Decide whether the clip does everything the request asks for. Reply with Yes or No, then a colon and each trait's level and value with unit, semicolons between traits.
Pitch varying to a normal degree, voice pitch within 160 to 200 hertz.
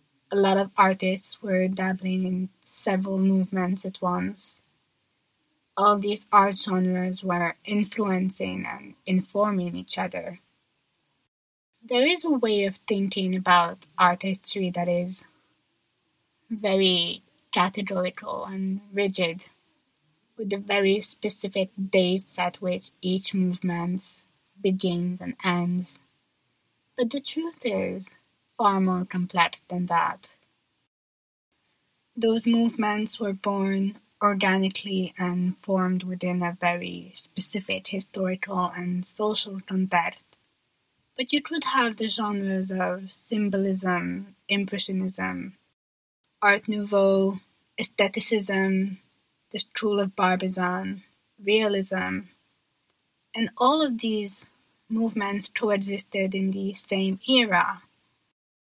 No: narrow, 2.2 semitones; high, 190 Hz